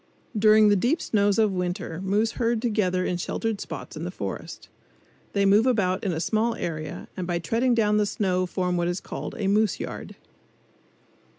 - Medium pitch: No, high, 200 Hz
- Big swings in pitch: No, average, 3.2 semitones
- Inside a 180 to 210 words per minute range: Yes, average, 185 wpm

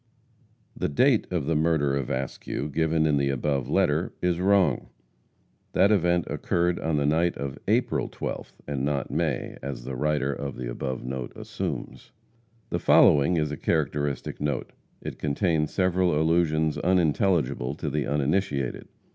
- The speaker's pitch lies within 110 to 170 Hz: No, very low, 75 Hz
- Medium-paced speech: Yes, average, 150 wpm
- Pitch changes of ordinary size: Yes, average, 3.6 semitones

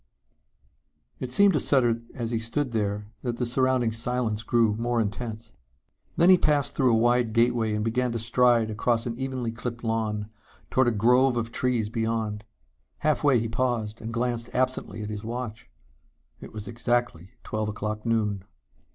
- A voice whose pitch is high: No, low, 115 Hz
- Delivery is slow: No, average, 170 wpm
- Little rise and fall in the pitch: Yes, narrow, 2.2 semitones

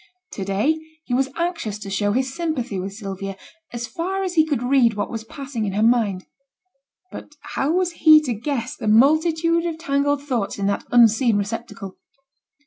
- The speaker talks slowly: No, average, 180 wpm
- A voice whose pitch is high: Yes, high, 245 Hz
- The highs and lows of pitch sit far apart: Yes, wide, 6.8 semitones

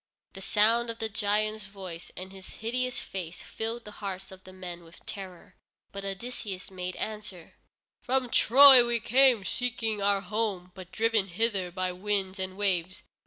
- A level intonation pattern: No, average, 3.3 semitones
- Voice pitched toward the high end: Yes, high, 200 Hz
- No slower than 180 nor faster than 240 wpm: No, average, 165 wpm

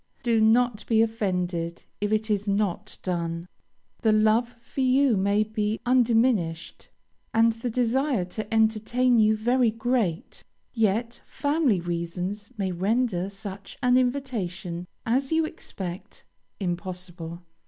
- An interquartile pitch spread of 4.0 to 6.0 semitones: Yes, average, 4.5 semitones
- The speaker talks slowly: Yes, slow, 120 wpm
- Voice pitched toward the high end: Yes, high, 215 Hz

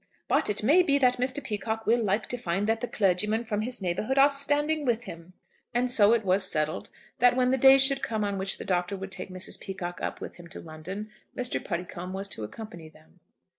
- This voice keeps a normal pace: No, fast, 225 wpm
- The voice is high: Yes, high, 215 Hz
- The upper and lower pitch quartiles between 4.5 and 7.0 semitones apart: Yes, average, 5.2 semitones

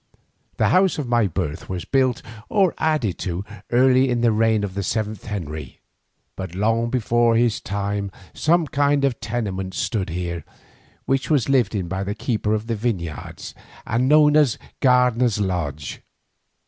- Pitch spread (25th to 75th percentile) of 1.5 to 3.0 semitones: No, average, 4.9 semitones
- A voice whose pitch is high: No, low, 115 Hz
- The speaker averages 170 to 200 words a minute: No, average, 160 wpm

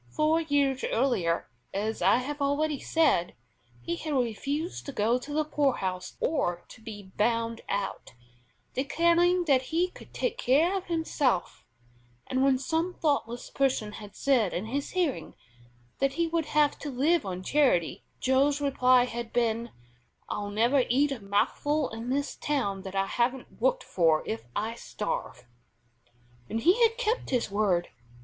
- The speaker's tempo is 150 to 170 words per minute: Yes, average, 155 wpm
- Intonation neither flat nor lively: No, wide, 5.8 semitones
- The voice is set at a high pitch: Yes, very high, 260 Hz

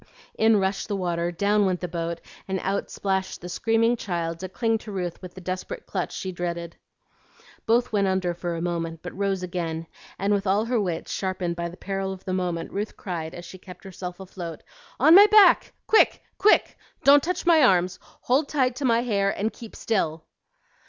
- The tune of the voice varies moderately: Yes, average, 3.9 semitones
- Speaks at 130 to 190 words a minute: No, average, 200 wpm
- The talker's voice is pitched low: No, high, 190 Hz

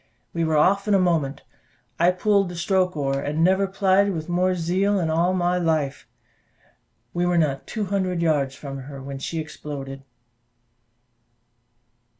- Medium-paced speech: Yes, average, 160 wpm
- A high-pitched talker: No, medium, 170 Hz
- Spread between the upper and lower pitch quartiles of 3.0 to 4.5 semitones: Yes, average, 3.9 semitones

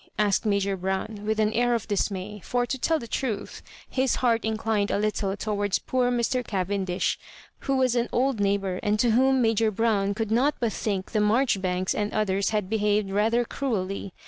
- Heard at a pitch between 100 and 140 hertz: No, high, 215 Hz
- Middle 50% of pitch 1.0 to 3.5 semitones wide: Yes, average, 3.0 semitones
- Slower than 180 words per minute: No, average, 185 wpm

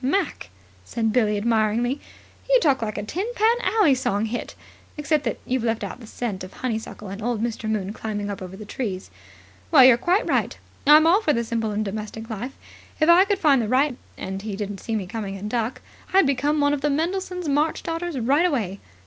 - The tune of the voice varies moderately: No, wide, 5.9 semitones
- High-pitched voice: Yes, high, 240 Hz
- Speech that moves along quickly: Yes, fast, 215 wpm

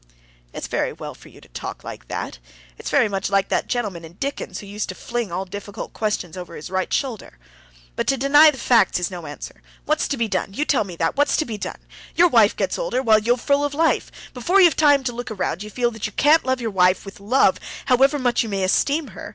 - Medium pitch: No, high, 225 Hz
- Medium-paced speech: No, fast, 240 wpm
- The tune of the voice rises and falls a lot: Yes, wide, 6.1 semitones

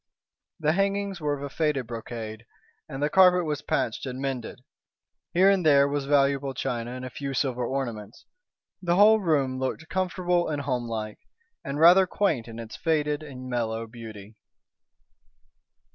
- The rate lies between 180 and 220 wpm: No, average, 155 wpm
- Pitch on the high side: No, medium, 140 Hz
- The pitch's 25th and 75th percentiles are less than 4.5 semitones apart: No, average, 5.1 semitones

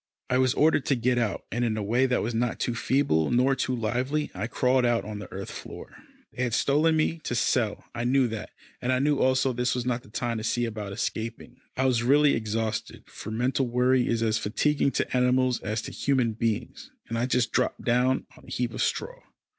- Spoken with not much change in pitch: Yes, narrow, 2.3 semitones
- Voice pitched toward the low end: Yes, low, 125 Hz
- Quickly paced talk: Yes, fast, 225 wpm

